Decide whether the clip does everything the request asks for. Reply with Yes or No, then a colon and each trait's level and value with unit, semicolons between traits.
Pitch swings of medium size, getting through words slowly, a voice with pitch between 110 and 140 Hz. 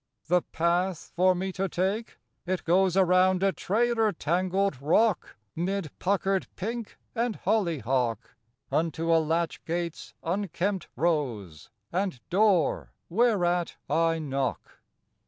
No: average, 3.0 semitones; slow, 115 wpm; medium, 180 Hz